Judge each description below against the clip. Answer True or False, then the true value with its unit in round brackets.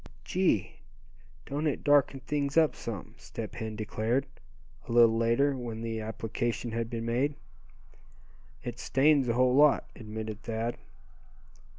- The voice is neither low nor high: False (120 Hz)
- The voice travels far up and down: False (3.6 semitones)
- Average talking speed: False (130 wpm)